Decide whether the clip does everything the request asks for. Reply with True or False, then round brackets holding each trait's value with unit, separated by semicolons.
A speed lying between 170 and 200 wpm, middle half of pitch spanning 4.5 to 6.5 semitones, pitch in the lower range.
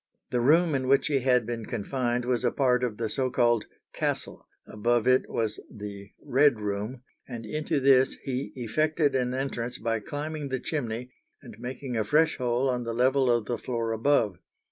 False (185 wpm; 2.8 semitones; 125 Hz)